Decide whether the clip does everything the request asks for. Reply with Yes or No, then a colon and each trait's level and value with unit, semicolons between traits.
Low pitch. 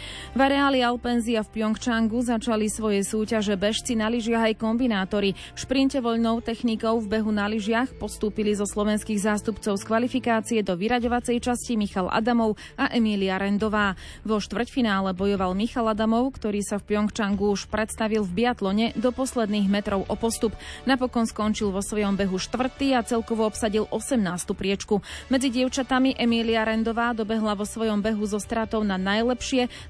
No: high, 220 Hz